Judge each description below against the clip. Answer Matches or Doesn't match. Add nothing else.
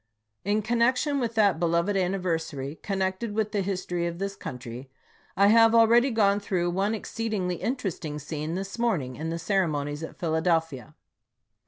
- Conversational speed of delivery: Matches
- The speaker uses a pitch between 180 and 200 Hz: Matches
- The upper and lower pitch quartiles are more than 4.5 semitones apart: Matches